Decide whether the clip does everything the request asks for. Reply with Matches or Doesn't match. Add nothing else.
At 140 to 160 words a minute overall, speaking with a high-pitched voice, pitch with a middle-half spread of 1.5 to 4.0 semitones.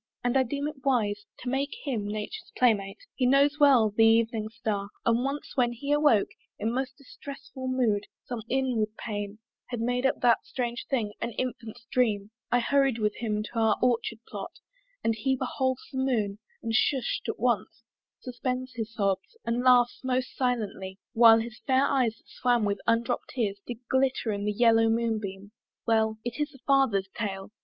Doesn't match